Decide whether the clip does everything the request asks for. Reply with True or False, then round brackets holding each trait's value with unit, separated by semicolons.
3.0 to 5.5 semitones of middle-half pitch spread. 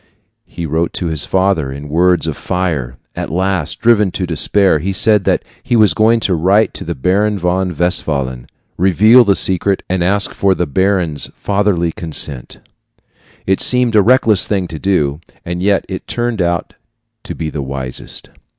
True (4.0 semitones)